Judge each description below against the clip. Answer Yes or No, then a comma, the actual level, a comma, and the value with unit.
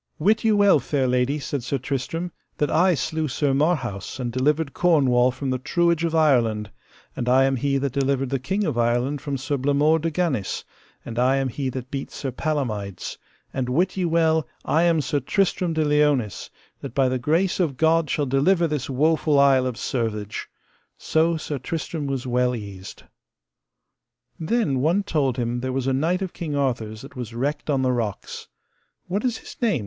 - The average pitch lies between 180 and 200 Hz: No, medium, 140 Hz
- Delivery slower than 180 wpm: No, average, 190 wpm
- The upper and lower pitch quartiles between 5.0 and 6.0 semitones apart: No, average, 4.1 semitones